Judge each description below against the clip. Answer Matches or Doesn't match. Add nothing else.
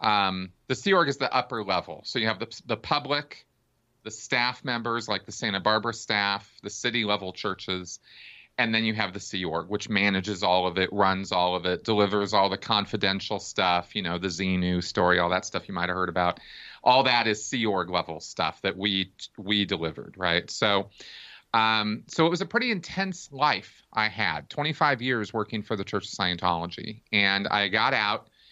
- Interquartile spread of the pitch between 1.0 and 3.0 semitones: Doesn't match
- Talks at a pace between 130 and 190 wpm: Doesn't match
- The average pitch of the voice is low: Matches